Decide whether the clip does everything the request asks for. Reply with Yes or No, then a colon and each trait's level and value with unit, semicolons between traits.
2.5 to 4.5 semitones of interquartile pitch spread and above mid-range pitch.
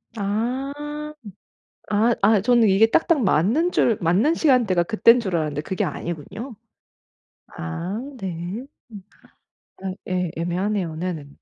No: average, 5.1 semitones; high, 200 Hz